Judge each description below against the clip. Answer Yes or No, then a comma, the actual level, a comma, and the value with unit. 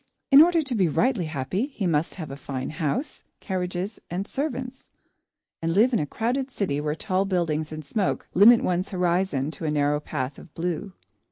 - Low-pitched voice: No, medium, 180 Hz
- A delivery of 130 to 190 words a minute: Yes, average, 185 wpm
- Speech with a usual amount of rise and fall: No, wide, 6.4 semitones